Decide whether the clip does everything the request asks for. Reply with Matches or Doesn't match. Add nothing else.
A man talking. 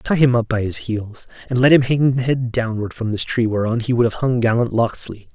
Matches